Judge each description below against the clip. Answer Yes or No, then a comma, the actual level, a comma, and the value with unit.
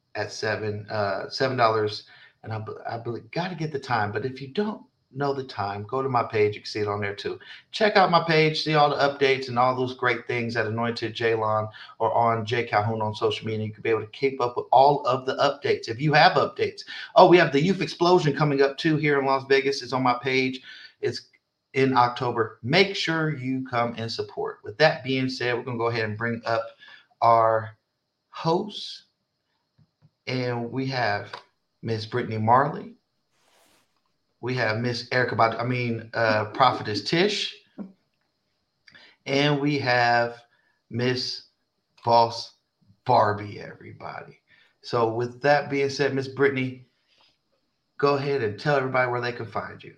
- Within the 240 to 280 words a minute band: No, average, 180 wpm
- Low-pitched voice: Yes, low, 125 Hz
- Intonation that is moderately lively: Yes, average, 4.0 semitones